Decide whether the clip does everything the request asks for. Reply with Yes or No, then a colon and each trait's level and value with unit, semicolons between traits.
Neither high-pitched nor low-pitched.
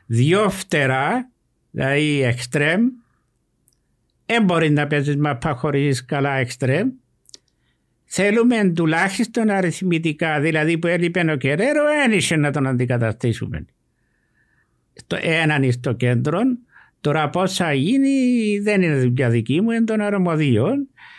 Yes: medium, 165 Hz